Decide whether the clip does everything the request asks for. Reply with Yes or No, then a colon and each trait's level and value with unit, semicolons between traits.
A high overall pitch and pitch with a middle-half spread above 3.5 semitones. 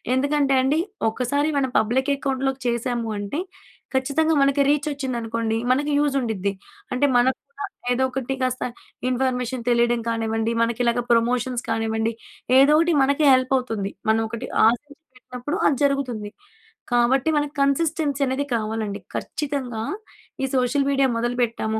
No: very high, 255 Hz; average, 3.2 semitones